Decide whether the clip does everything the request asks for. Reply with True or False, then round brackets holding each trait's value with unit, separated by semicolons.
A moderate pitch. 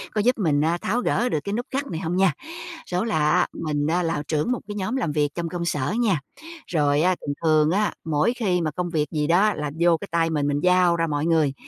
True (170 Hz)